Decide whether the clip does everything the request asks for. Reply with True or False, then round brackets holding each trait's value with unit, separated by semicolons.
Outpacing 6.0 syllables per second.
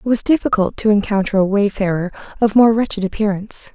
True (6.2 syllables/s)